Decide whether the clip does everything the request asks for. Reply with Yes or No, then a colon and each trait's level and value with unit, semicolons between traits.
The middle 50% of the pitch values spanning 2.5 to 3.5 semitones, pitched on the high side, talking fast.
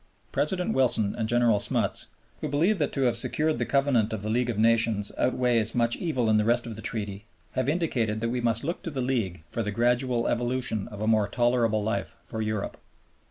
No: average, 2.8 semitones; low, 115 Hz; fast, 210 wpm